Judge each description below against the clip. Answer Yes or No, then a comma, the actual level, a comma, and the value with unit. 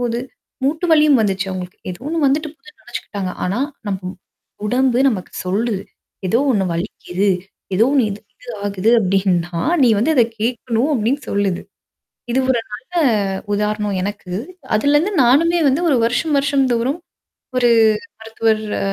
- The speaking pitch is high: Yes, high, 225 Hz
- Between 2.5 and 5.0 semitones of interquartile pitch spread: No, wide, 5.5 semitones